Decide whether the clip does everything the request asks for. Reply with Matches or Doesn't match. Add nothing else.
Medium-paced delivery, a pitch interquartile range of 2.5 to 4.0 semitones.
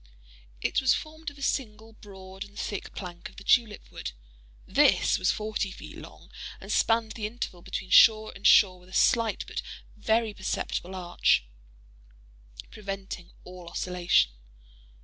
Matches